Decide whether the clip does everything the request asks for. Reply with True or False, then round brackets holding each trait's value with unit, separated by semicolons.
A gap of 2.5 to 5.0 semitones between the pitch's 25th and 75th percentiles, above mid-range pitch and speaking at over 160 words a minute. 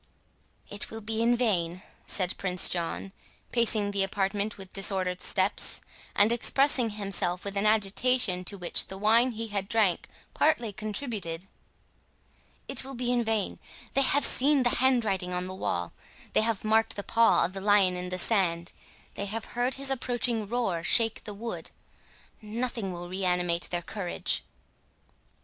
False (3.9 semitones; 205 Hz; 145 wpm)